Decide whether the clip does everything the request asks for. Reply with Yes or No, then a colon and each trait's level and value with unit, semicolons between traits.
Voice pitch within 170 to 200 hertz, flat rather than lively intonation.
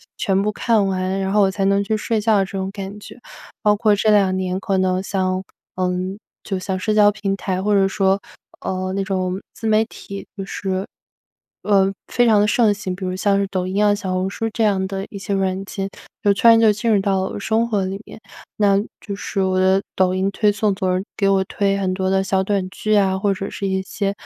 Yes: high, 195 Hz; narrow, 1.5 semitones